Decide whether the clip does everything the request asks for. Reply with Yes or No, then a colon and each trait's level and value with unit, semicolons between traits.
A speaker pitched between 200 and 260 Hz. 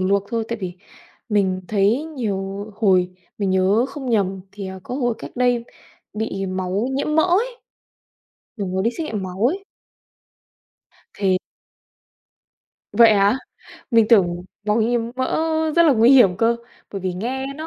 Yes: high, 210 Hz